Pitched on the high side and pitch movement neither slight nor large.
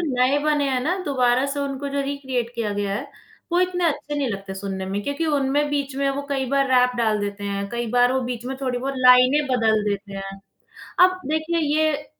Yes: very high, 260 Hz; average, 4.1 semitones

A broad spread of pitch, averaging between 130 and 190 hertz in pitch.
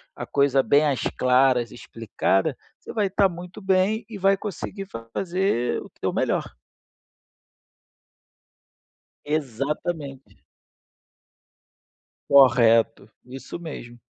Yes: wide, 6.9 semitones; medium, 140 Hz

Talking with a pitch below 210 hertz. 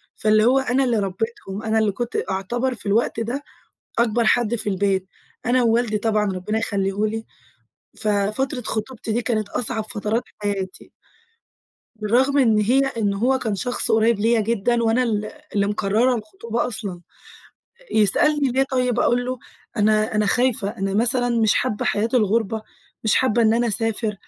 No: high, 225 Hz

